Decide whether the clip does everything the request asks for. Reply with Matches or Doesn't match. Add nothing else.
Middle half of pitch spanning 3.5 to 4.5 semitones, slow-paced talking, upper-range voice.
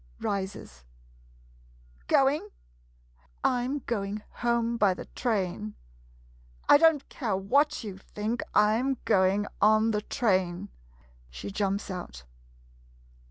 Matches